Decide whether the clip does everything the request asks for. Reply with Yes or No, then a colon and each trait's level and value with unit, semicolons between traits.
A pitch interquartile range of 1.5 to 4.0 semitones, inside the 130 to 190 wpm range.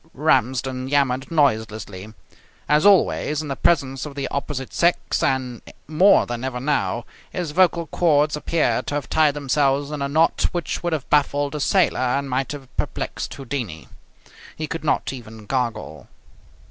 Yes: average, 3.2 semitones; average, 160 wpm